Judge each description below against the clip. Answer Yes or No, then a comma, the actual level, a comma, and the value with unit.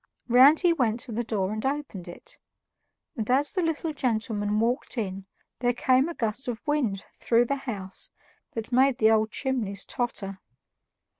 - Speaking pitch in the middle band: No, high, 240 Hz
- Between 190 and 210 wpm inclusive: No, average, 165 wpm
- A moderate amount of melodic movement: Yes, average, 3.9 semitones